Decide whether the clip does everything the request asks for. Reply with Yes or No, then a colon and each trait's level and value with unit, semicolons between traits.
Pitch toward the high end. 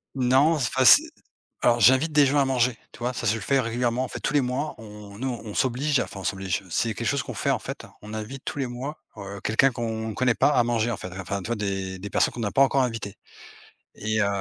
No: low, 120 Hz